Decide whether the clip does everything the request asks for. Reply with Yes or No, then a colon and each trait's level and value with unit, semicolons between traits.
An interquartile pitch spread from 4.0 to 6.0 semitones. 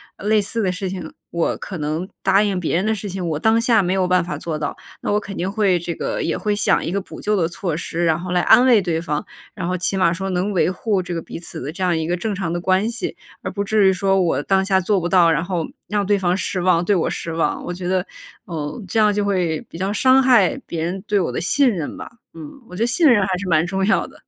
No: average, 3.0 semitones